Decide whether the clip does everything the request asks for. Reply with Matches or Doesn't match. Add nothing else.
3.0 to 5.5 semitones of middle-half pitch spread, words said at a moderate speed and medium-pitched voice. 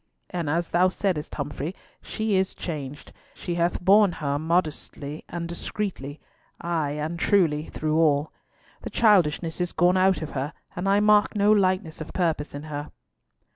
Matches